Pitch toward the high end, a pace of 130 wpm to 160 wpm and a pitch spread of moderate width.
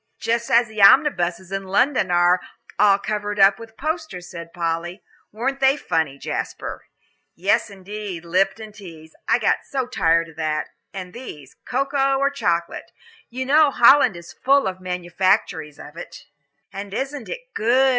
No: high, 200 Hz; average, 155 wpm; wide, 6.6 semitones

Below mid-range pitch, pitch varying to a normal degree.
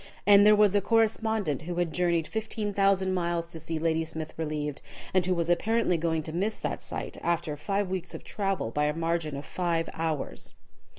No: medium, 170 Hz; average, 3.6 semitones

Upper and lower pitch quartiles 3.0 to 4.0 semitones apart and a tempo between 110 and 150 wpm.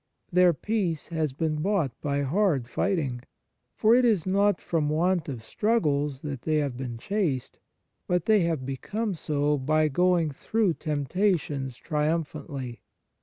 No: average, 4.8 semitones; average, 140 wpm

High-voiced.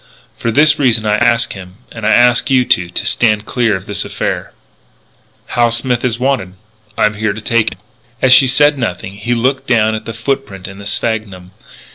No: low, 115 Hz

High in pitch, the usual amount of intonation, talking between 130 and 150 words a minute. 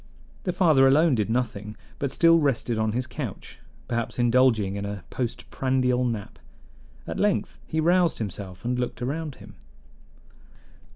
No: low, 125 Hz; average, 4.3 semitones; average, 140 wpm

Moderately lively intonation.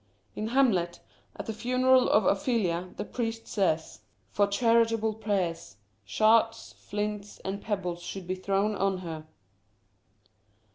Yes: average, 3.9 semitones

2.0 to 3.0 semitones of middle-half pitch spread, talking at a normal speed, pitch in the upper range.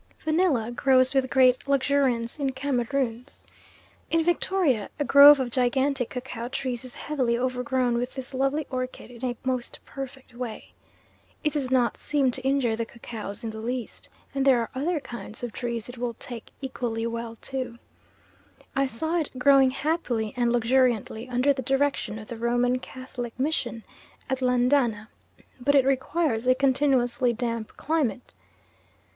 Yes: narrow, 2.4 semitones; average, 155 wpm; very high, 255 Hz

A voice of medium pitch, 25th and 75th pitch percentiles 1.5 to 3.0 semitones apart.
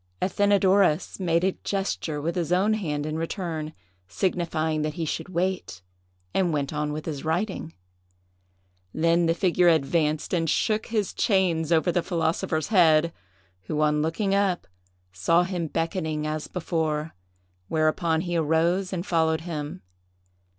Yes: medium, 165 Hz; average, 2.7 semitones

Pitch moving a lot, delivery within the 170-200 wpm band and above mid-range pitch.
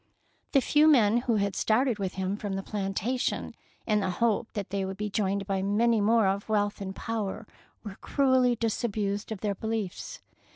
No: average, 2.7 semitones; average, 180 wpm; high, 210 Hz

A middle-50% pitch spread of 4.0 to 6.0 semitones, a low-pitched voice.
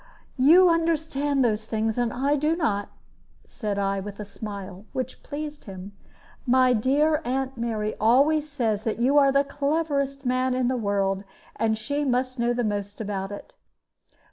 No: average, 5.0 semitones; very high, 250 Hz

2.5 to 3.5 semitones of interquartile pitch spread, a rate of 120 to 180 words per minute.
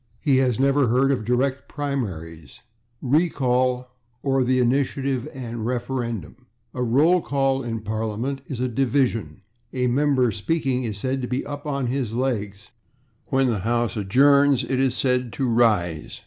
Yes: average, 2.8 semitones; average, 160 wpm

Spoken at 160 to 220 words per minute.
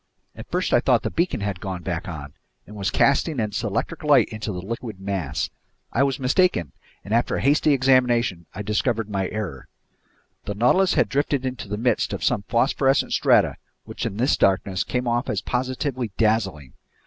Yes: average, 185 wpm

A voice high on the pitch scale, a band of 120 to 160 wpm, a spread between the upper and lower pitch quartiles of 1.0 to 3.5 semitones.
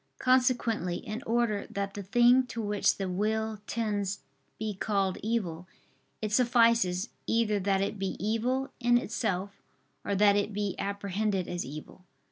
Yes: high, 210 Hz; average, 145 wpm; average, 2.9 semitones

